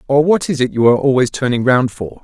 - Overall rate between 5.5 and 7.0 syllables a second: Yes, 6.3 syllables/s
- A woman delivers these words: No, male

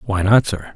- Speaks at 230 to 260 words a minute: Yes, fast, 240 wpm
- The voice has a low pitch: Yes, low, 105 Hz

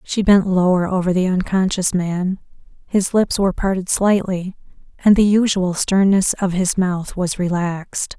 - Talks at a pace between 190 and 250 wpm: No, average, 155 wpm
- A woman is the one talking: Yes, female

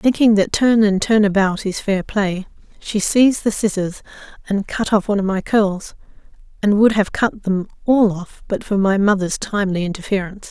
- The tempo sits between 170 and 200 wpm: Yes, average, 190 wpm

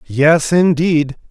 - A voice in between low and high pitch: Yes, medium, 155 Hz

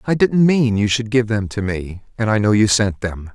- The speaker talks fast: Yes, fast, 270 wpm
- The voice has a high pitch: No, low, 110 Hz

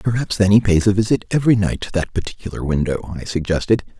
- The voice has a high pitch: No, low, 100 Hz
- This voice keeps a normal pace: No, fast, 210 wpm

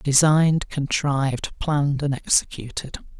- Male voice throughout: Yes, male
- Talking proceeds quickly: No, slow, 95 wpm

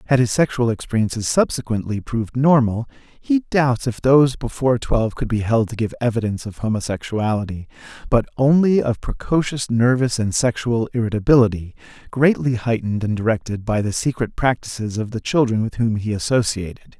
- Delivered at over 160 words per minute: No, average, 155 wpm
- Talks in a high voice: No, low, 115 Hz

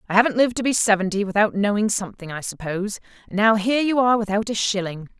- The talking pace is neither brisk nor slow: No, fast, 220 wpm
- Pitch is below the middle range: No, high, 210 Hz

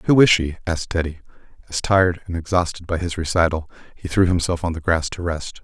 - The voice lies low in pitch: Yes, very low, 85 Hz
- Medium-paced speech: No, fast, 215 wpm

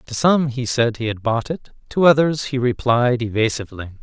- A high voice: No, low, 125 Hz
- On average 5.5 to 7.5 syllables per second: No, 5.0 syllables/s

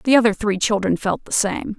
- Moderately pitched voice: No, high, 215 Hz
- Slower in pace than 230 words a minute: No, fast, 235 wpm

